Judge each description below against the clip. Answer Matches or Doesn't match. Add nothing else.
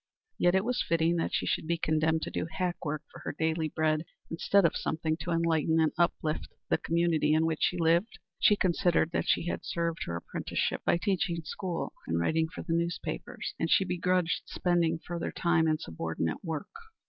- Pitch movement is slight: Matches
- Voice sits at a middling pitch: Matches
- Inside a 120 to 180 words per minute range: Doesn't match